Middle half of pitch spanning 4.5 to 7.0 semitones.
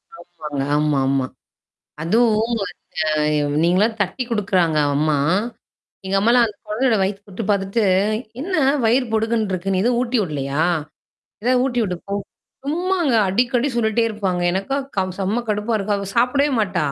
Yes: average, 5.2 semitones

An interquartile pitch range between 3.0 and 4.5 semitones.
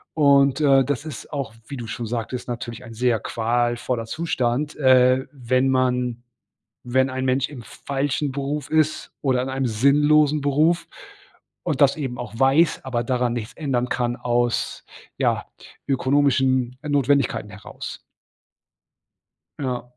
No: narrow, 2.6 semitones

